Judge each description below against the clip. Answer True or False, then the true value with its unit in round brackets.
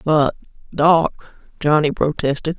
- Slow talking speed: True (95 wpm)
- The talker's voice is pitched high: False (155 Hz)